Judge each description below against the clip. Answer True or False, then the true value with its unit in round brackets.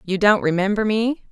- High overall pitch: True (205 Hz)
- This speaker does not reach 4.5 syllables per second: False (5.3 syllables/s)